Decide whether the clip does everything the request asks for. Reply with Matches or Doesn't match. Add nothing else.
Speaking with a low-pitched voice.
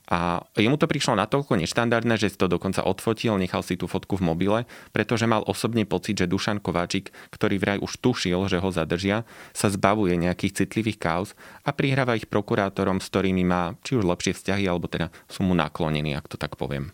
Matches